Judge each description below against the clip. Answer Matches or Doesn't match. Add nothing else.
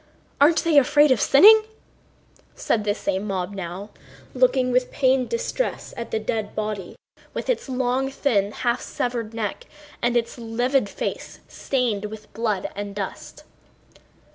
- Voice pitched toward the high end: Matches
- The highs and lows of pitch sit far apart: Doesn't match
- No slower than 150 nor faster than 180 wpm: Doesn't match